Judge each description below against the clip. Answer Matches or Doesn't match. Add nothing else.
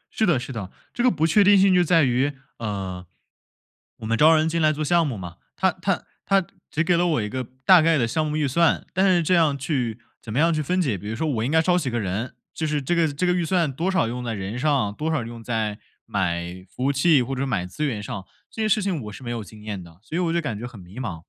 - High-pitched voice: Doesn't match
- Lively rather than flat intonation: Matches